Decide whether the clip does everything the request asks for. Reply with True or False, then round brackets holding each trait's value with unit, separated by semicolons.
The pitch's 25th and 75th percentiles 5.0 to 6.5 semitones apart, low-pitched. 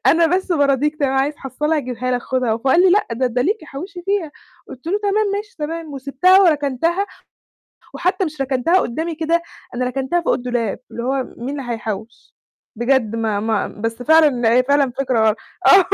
False (5.3 semitones; 275 Hz)